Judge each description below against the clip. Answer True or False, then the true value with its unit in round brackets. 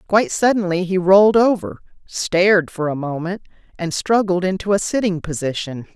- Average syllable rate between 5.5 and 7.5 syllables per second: False (5.2 syllables/s)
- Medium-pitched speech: True (180 Hz)